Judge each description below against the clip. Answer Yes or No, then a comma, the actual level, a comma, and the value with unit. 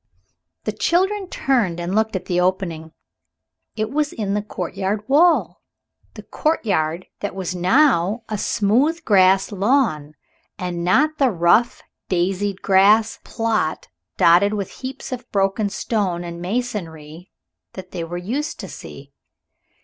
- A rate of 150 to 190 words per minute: No, slow, 135 wpm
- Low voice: No, high, 200 Hz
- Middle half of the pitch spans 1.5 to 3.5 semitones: No, average, 5.1 semitones